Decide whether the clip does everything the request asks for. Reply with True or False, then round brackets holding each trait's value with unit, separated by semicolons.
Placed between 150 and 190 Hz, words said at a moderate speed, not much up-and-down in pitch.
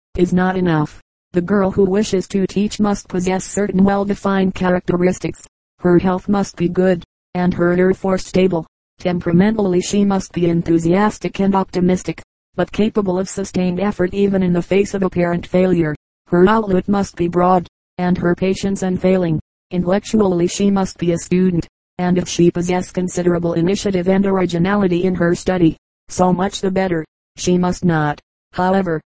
True (185 Hz; 160 wpm; 1.6 semitones)